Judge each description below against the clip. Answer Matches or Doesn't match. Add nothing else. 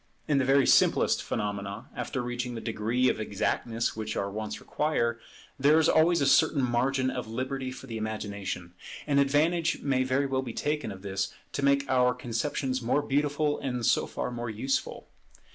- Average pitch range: Matches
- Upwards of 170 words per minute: Matches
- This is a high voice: Doesn't match